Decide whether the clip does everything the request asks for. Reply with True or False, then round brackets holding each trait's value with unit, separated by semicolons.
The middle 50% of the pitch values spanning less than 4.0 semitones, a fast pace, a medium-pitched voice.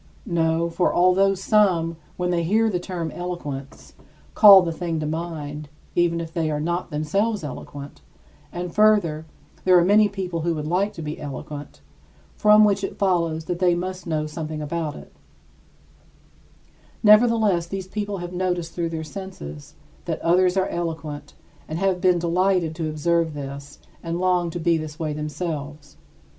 False (3.0 semitones; 160 wpm; 170 Hz)